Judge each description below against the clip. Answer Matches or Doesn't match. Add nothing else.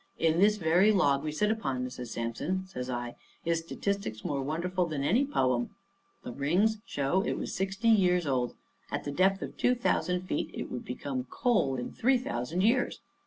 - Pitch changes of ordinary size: Doesn't match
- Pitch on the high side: Doesn't match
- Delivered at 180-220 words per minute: Matches